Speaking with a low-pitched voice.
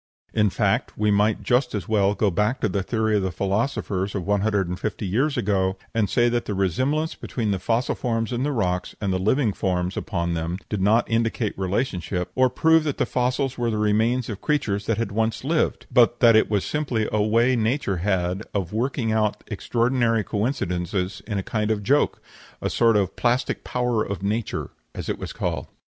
Yes: low, 110 Hz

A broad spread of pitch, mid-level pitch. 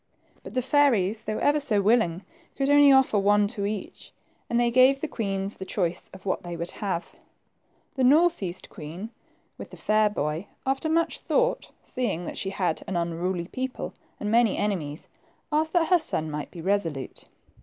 No: wide, 6.6 semitones; high, 210 Hz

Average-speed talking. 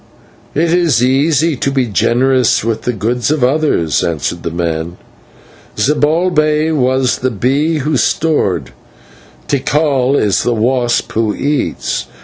No: slow, 130 wpm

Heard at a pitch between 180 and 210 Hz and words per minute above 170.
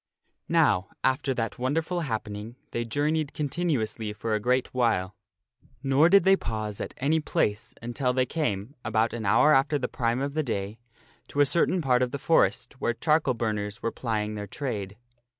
No: low, 125 Hz; average, 185 wpm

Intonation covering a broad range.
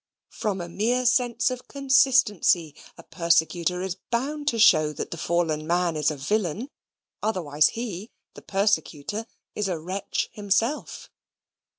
Yes: wide, 5.8 semitones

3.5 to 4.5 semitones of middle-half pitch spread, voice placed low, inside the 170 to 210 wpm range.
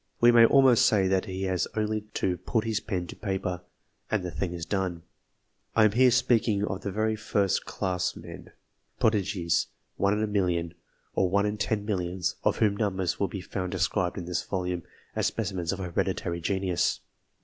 No: average, 3.0 semitones; very low, 95 Hz; average, 180 wpm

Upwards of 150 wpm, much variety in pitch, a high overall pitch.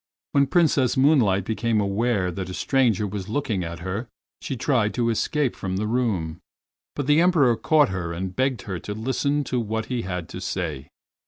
No: average, 185 wpm; wide, 5.7 semitones; low, 110 Hz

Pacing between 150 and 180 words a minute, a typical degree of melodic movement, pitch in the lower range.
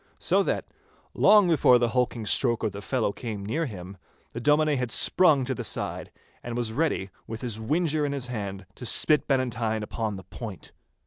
No: average, 190 wpm; average, 4.6 semitones; low, 120 Hz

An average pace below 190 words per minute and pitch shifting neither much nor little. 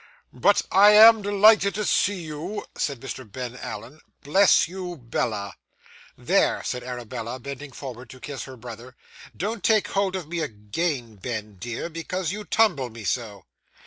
No: average, 155 wpm; wide, 7.9 semitones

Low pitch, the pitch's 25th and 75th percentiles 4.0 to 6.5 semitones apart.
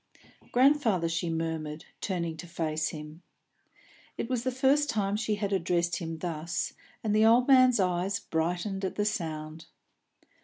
No: medium, 180 Hz; average, 5.0 semitones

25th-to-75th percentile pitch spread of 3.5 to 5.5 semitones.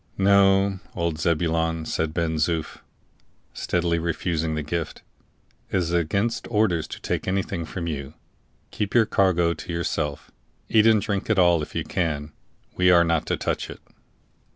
No: average, 3.1 semitones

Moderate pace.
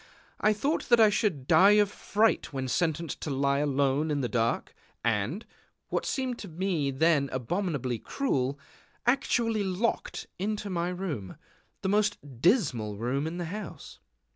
Yes: average, 150 wpm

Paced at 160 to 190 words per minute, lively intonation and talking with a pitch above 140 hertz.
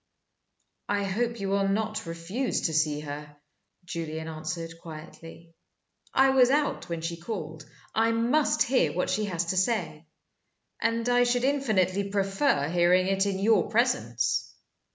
No: average, 145 wpm; wide, 5.7 semitones; high, 190 Hz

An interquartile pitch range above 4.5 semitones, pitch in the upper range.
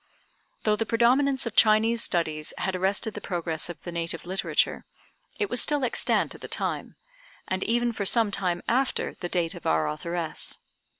Yes: average, 5.2 semitones; high, 195 Hz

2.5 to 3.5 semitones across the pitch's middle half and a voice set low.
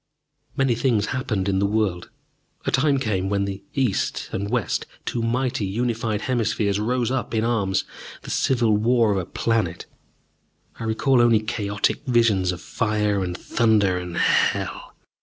Yes: average, 3.2 semitones; low, 110 Hz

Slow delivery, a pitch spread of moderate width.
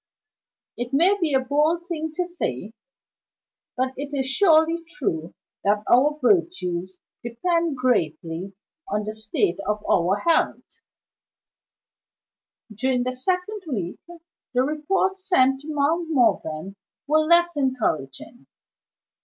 No: slow, 115 wpm; wide, 7.9 semitones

